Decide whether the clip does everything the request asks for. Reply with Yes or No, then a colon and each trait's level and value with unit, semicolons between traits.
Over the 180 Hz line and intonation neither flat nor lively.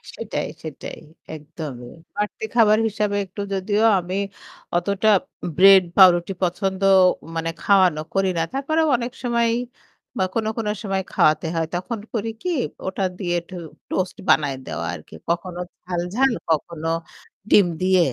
Yes: high, 190 Hz; average, 3.6 semitones